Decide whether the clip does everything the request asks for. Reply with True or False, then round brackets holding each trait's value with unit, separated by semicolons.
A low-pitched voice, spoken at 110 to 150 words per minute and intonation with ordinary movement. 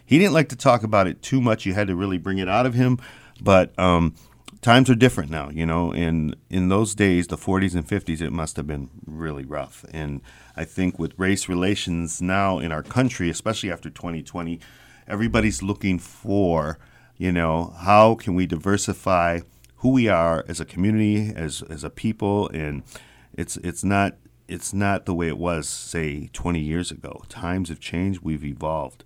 False (90 Hz; 190 wpm; 3.7 semitones)